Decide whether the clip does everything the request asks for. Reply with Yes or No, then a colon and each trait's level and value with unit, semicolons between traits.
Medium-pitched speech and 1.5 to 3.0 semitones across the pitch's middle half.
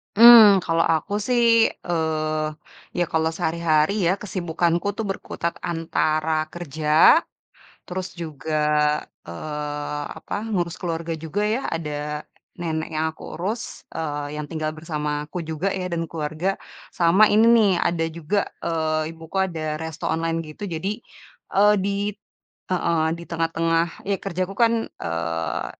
Yes: medium, 165 Hz; average, 2.7 semitones